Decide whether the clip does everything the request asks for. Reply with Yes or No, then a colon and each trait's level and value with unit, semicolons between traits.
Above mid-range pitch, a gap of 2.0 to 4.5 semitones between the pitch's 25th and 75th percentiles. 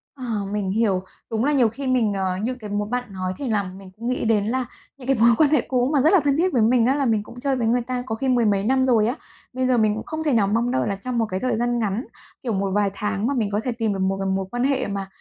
Yes: high, 230 Hz; average, 3.8 semitones